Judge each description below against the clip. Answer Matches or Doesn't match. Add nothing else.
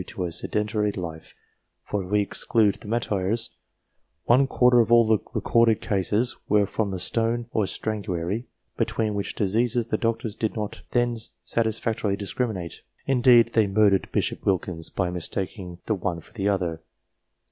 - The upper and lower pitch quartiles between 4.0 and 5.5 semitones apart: Doesn't match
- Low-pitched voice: Matches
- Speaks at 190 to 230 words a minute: Doesn't match